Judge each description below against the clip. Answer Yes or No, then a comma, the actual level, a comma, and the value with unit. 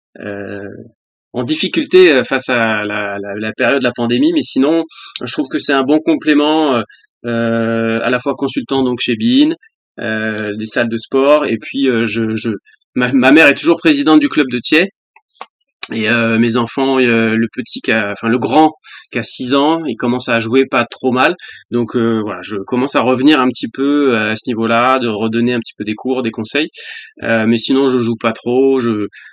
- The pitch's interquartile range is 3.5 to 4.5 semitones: Yes, average, 4.2 semitones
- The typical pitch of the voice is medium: No, low, 125 Hz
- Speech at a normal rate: Yes, average, 210 wpm